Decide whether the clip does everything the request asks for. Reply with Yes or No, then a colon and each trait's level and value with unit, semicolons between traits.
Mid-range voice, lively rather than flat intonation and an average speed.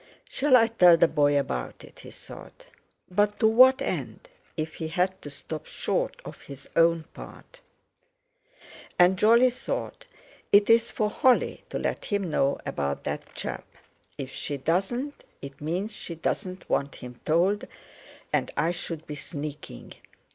Yes: medium, 180 Hz; wide, 6.7 semitones; average, 145 wpm